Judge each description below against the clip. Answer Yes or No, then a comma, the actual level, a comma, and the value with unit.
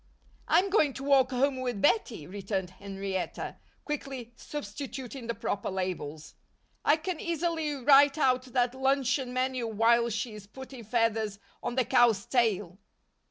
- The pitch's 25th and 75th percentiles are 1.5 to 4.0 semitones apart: No, average, 4.4 semitones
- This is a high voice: Yes, high, 245 Hz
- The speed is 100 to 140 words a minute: Yes, slow, 135 wpm